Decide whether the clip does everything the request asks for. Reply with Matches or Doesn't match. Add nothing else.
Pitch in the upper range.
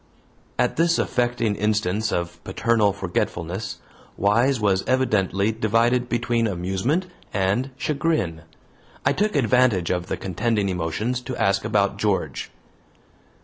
Doesn't match